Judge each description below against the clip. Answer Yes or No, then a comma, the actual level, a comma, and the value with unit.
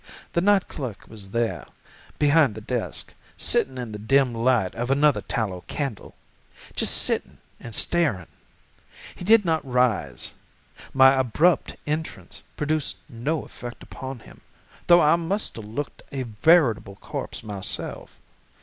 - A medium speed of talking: No, slow, 130 wpm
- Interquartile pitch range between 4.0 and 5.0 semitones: No, wide, 5.6 semitones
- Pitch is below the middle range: Yes, low, 130 Hz